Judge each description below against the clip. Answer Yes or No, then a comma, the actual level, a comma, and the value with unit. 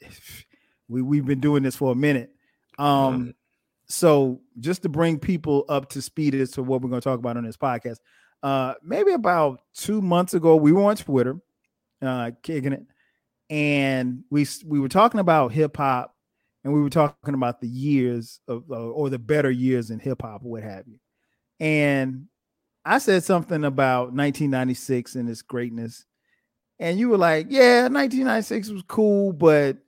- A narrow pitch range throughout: No, average, 4.6 semitones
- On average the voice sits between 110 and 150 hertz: Yes, medium, 140 Hz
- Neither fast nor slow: Yes, average, 170 wpm